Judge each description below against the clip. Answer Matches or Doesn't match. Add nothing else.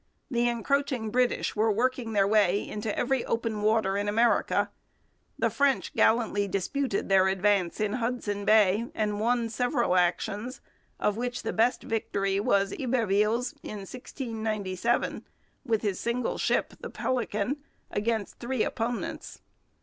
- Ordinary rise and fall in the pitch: Matches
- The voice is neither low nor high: Doesn't match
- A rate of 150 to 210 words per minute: Doesn't match